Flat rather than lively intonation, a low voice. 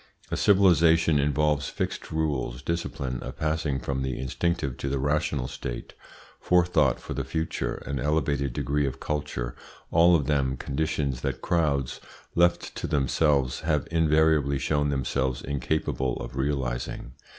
No: average, 3.0 semitones; very low, 70 Hz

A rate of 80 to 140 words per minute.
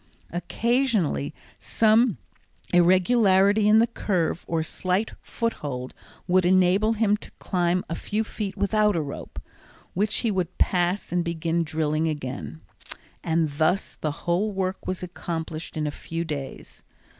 Yes: slow, 135 wpm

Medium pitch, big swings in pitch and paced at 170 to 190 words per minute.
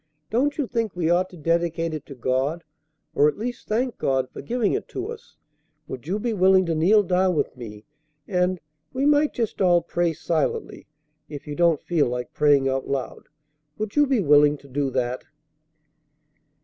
Yes: medium, 170 Hz; wide, 6.8 semitones; average, 185 wpm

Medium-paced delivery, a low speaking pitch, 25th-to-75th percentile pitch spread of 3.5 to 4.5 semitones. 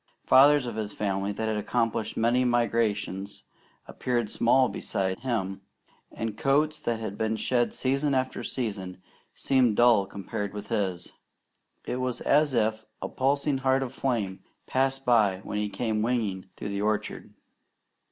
Yes: average, 150 wpm; low, 115 Hz; average, 4.0 semitones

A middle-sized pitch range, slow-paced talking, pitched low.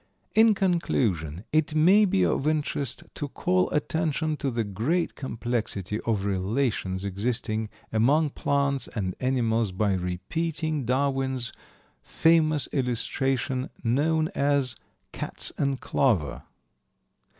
No: wide, 5.7 semitones; slow, 105 wpm; low, 130 Hz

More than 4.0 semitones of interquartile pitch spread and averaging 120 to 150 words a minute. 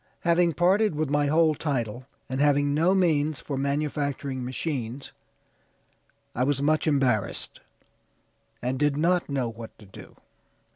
No: average, 3.1 semitones; slow, 135 wpm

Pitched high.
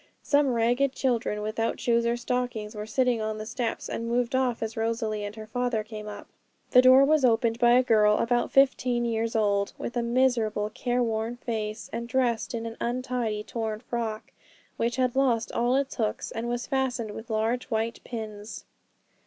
Yes: high, 235 Hz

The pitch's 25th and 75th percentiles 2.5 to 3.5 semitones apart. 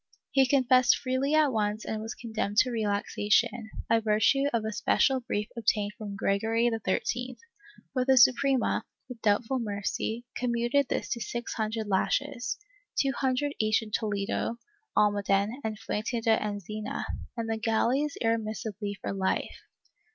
Yes: average, 3.2 semitones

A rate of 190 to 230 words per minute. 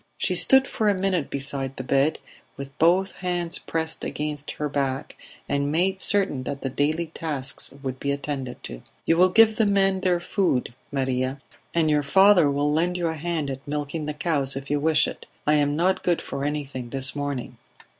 Yes: average, 195 wpm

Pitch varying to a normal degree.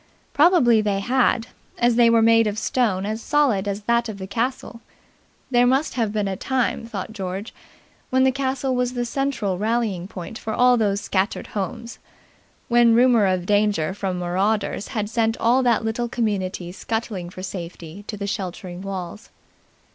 Yes: average, 3.6 semitones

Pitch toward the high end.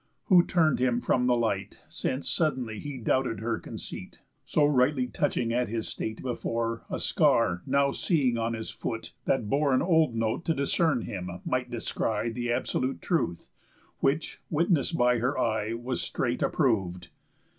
No: low, 125 Hz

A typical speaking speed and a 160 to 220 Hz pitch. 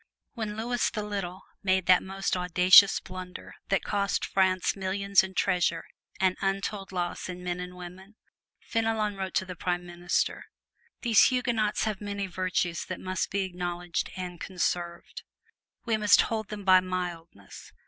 Yes: average, 150 wpm; medium, 185 Hz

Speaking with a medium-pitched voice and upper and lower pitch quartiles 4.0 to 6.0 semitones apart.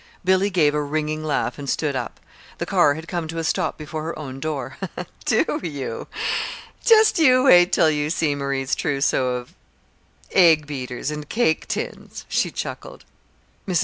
No: medium, 155 Hz; average, 3.6 semitones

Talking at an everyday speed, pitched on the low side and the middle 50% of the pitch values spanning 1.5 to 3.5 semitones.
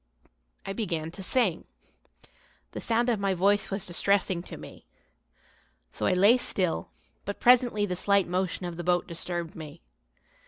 No: average, 155 wpm; high, 190 Hz; average, 2.9 semitones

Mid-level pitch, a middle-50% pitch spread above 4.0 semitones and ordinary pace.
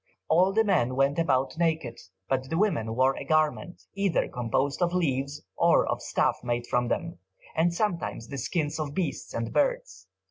Yes: medium, 145 Hz; average, 5.0 semitones; average, 175 wpm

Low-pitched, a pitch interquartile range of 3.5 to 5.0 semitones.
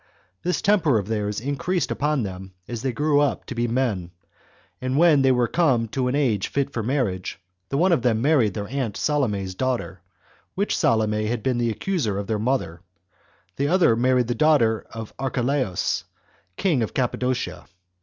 Yes: low, 125 Hz; average, 4.6 semitones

